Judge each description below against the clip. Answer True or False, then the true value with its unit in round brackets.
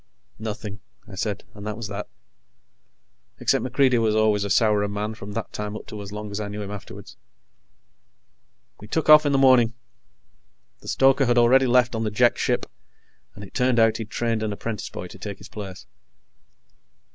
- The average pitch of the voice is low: True (110 Hz)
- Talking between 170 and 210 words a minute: True (190 wpm)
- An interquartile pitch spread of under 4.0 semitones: True (2.8 semitones)